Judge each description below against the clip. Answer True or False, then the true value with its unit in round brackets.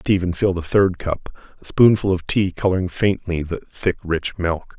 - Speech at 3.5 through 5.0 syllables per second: True (4.9 syllables/s)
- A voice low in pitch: True (90 Hz)